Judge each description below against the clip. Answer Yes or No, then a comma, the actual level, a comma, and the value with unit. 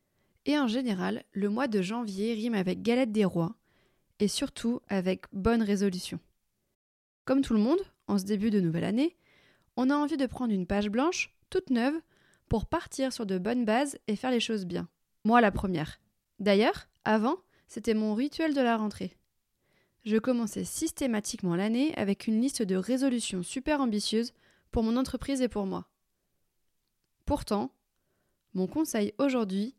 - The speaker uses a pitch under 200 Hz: No, high, 230 Hz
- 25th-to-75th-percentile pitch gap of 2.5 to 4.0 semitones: No, average, 4.4 semitones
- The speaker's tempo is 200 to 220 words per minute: No, average, 160 wpm